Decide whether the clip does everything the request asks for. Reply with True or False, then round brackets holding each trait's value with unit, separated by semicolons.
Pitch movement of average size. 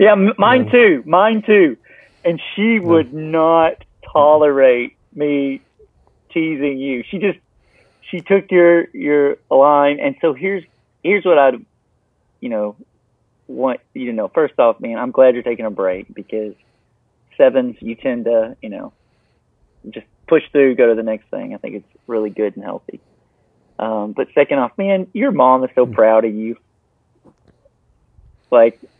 False (8.1 semitones)